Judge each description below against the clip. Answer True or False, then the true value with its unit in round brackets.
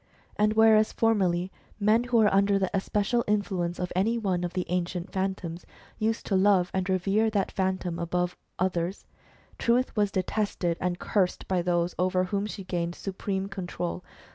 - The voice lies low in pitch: False (190 Hz)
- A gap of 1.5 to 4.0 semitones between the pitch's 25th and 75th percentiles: True (2.7 semitones)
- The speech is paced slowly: False (165 wpm)